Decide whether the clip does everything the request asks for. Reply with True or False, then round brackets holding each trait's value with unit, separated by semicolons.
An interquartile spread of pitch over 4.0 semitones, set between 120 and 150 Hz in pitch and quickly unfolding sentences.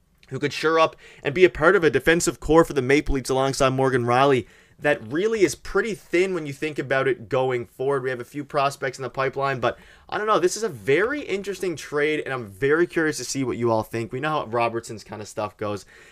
True (4.6 semitones; 140 Hz; 250 wpm)